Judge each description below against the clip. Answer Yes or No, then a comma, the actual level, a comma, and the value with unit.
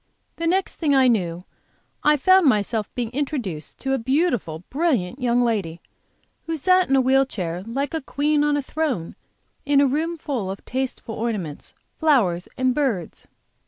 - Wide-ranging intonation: Yes, wide, 5.9 semitones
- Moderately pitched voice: No, very high, 260 Hz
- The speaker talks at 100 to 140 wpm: No, average, 165 wpm